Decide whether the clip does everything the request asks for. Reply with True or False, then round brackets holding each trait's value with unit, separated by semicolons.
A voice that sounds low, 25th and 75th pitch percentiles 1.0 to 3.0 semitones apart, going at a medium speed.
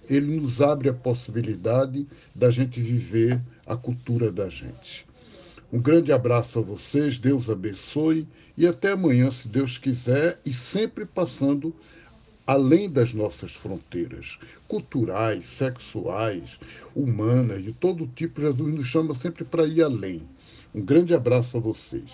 False (130 Hz; 5.0 semitones; 135 wpm)